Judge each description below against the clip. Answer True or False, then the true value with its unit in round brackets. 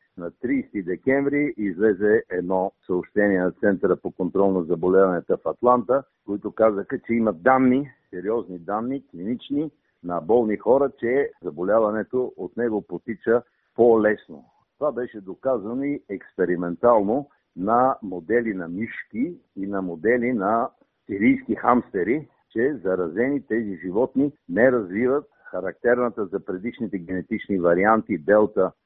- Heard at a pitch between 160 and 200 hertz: False (110 Hz)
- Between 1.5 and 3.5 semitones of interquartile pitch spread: False (5.3 semitones)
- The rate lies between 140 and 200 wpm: False (125 wpm)